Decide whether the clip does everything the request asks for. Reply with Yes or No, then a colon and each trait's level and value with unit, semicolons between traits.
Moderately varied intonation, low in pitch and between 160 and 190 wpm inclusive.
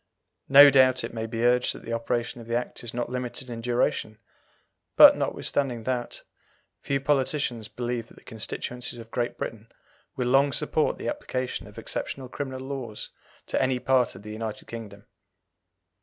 No: narrow, 2.1 semitones; low, 120 Hz; average, 170 wpm